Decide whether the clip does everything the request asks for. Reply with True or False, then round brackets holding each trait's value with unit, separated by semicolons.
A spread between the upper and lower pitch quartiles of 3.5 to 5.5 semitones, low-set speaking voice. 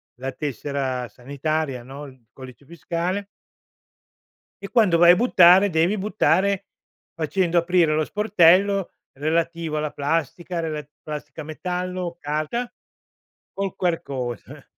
False (4.0 semitones; 165 Hz)